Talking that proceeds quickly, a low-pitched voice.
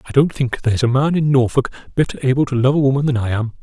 Yes: fast, 280 wpm; low, 130 Hz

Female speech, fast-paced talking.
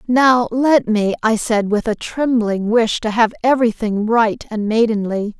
No: female; average, 180 wpm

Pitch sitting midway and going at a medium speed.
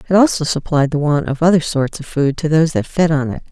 No: medium, 155 Hz; fast, 275 wpm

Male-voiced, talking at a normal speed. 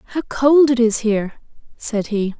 No: female; average, 175 wpm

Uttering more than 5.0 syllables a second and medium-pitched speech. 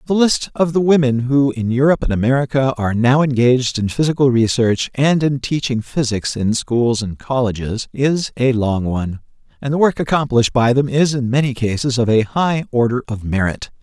No: 5.3 syllables/s; low, 125 Hz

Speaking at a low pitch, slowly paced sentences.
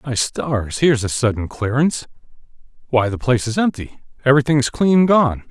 Yes: low, 125 Hz; slow, 130 wpm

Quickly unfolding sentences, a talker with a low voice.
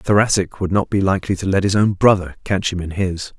Yes: fast, 265 wpm; very low, 95 Hz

